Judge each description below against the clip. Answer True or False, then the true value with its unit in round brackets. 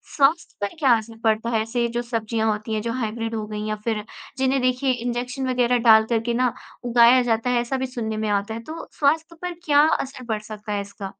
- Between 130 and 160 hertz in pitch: False (235 Hz)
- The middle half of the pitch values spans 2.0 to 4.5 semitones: True (2.5 semitones)